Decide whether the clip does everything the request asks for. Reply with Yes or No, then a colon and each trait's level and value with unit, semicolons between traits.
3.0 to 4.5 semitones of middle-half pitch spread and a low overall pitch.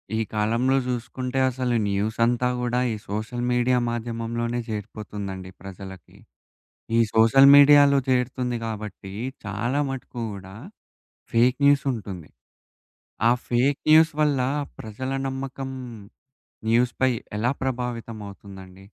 Yes: average, 3.4 semitones; low, 120 Hz